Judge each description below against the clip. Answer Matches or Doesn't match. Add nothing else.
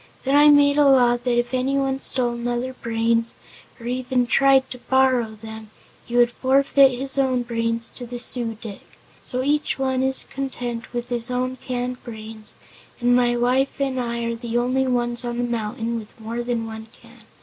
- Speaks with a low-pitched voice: Doesn't match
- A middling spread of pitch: Doesn't match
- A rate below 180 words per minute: Doesn't match